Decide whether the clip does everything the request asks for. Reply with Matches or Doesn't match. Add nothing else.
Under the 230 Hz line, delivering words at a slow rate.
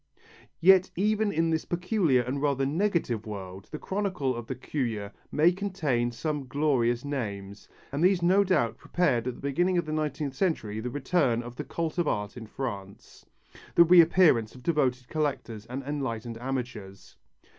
Doesn't match